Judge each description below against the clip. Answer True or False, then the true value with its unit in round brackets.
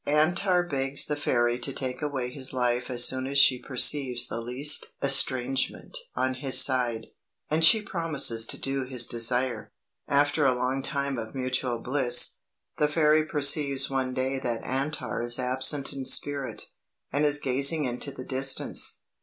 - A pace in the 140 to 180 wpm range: True (160 wpm)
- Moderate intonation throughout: False (2.2 semitones)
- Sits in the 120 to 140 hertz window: True (135 Hz)